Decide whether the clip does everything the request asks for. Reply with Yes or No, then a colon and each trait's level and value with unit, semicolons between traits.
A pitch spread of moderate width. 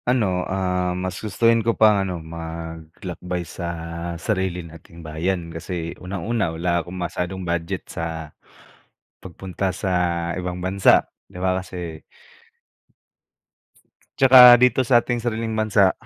Yes: average, 3.2 semitones